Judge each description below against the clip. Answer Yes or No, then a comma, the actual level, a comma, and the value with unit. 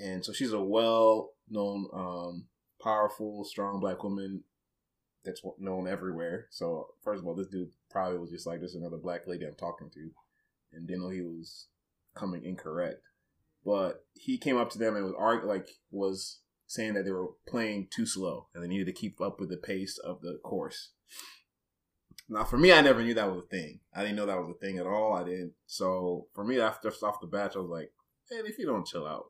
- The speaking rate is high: Yes, fast, 215 wpm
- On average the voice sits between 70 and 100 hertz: Yes, very low, 95 Hz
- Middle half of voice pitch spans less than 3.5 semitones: Yes, average, 2.9 semitones